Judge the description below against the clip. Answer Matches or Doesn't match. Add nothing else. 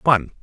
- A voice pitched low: Matches